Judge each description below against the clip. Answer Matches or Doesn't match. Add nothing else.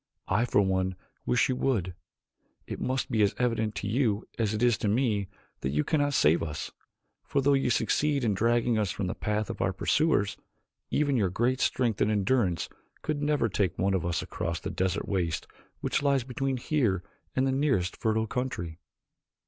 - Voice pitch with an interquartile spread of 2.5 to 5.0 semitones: Doesn't match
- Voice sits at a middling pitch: Doesn't match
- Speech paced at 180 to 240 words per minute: Matches